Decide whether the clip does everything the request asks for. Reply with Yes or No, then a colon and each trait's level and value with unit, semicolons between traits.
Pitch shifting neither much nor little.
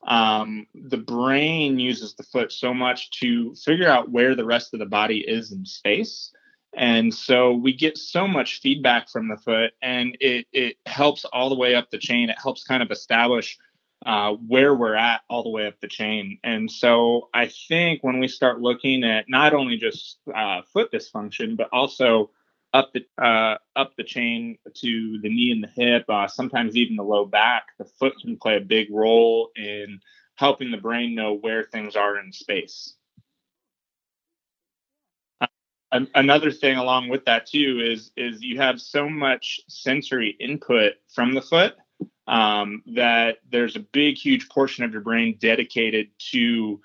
Yes: average, 3.7 semitones